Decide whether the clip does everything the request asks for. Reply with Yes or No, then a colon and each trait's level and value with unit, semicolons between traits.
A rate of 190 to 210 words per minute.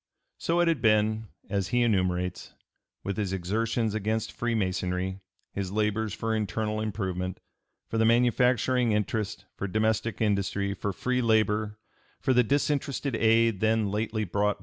No: average, 145 wpm